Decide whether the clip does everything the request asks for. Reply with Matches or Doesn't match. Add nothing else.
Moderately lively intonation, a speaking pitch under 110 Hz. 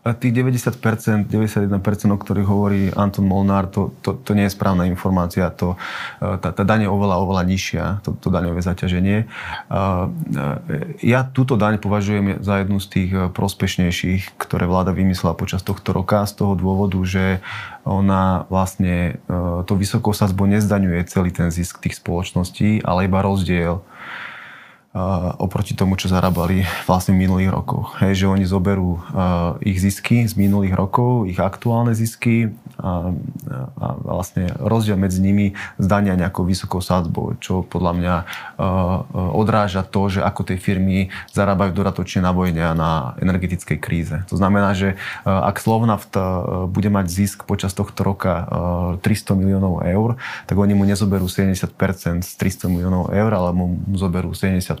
Doesn't match